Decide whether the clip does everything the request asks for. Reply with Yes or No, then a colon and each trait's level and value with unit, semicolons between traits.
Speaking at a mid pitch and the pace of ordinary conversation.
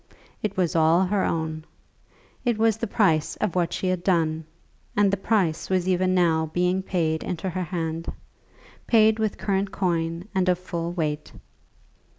Yes: medium, 180 Hz; average, 165 wpm